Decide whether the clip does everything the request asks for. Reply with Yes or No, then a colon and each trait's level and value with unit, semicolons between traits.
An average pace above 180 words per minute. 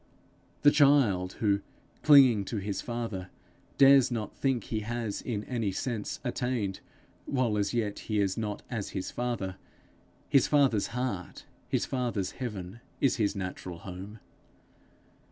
No: slow, 135 wpm